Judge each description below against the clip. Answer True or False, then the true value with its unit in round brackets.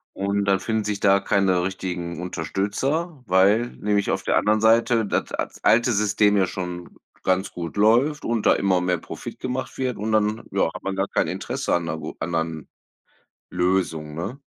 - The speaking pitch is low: True (100 Hz)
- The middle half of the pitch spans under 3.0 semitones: False (3.4 semitones)